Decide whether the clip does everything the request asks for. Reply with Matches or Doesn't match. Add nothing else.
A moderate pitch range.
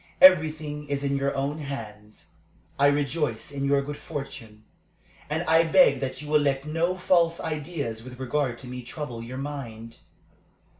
Matches